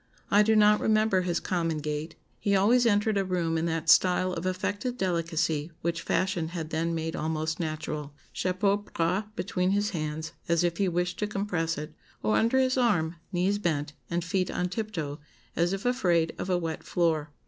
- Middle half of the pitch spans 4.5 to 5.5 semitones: No, average, 3.6 semitones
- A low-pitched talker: No, medium, 175 Hz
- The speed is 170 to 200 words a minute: Yes, average, 185 wpm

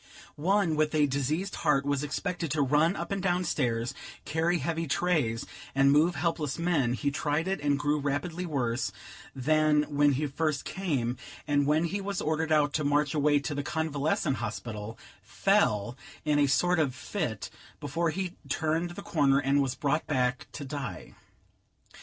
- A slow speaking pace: No, average, 170 wpm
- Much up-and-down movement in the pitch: No, average, 3.1 semitones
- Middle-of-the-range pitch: Yes, medium, 150 Hz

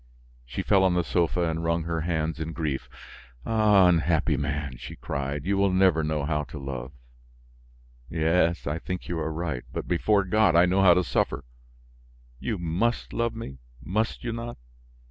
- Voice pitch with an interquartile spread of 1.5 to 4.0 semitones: Yes, average, 3.5 semitones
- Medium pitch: No, very low, 85 Hz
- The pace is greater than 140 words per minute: Yes, average, 175 wpm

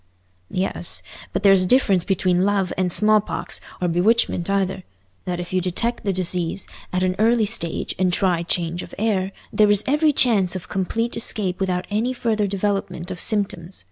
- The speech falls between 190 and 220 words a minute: No, average, 170 wpm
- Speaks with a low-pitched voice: No, high, 190 Hz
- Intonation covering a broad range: No, average, 2.9 semitones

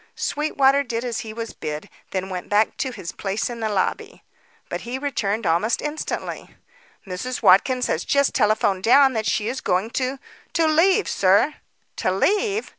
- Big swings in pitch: Yes, wide, 5.7 semitones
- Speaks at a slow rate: No, average, 170 wpm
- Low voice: No, high, 230 Hz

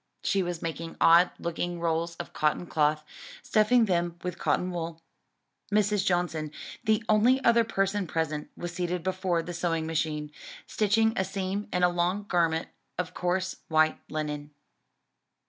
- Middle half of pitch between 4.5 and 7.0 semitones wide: No, average, 2.9 semitones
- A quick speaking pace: No, average, 145 wpm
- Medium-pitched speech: Yes, medium, 175 Hz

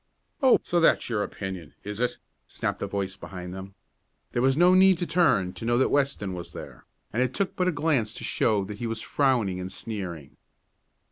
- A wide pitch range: Yes, wide, 6.8 semitones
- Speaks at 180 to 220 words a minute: Yes, fast, 205 wpm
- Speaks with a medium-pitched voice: No, low, 115 Hz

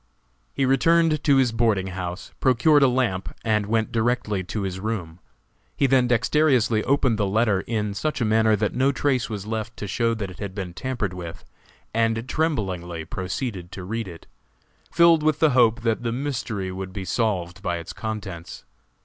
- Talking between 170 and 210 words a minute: Yes, average, 180 wpm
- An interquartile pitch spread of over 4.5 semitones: Yes, average, 4.9 semitones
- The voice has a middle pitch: No, low, 110 Hz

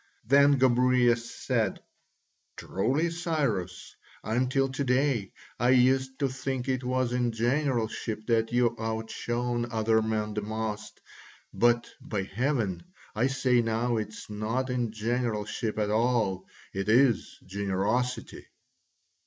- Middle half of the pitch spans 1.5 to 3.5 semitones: Yes, average, 2.8 semitones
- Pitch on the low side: Yes, low, 120 Hz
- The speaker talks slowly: Yes, slow, 120 wpm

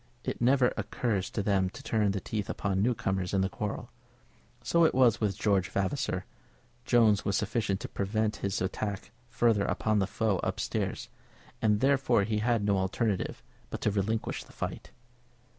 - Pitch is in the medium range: No, low, 105 Hz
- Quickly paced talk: No, average, 170 wpm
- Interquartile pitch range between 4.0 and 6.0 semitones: No, average, 2.8 semitones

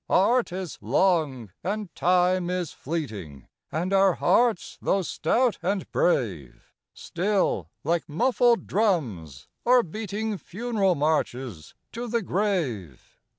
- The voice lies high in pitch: No, medium, 180 Hz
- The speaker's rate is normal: No, slow, 110 wpm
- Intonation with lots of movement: Yes, wide, 7.1 semitones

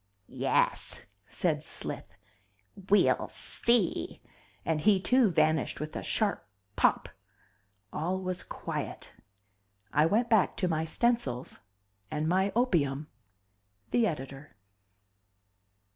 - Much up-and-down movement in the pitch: Yes, wide, 5.8 semitones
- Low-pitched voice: No, medium, 180 Hz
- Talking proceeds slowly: Yes, slow, 100 wpm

